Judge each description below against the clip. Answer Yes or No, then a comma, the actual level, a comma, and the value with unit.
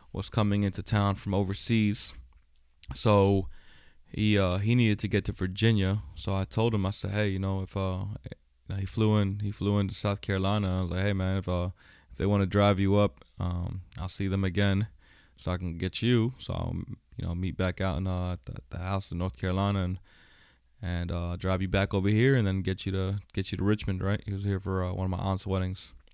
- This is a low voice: Yes, very low, 95 Hz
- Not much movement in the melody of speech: Yes, narrow, 1.8 semitones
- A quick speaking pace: Yes, fast, 230 wpm